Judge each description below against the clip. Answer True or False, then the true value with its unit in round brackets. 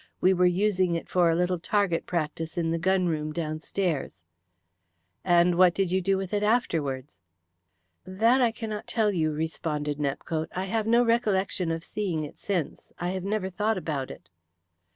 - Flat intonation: False (3.7 semitones)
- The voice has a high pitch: False (180 Hz)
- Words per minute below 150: False (170 wpm)